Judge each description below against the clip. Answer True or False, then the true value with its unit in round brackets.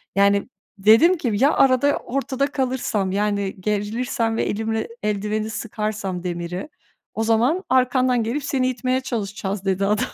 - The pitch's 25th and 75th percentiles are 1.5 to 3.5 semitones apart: False (4.1 semitones)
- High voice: True (220 Hz)